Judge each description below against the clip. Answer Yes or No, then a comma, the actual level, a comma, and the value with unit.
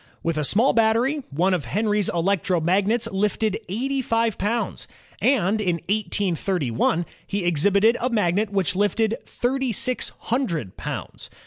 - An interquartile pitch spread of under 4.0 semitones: No, average, 4.3 semitones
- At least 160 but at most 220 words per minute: No, slow, 135 wpm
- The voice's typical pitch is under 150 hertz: No, high, 205 Hz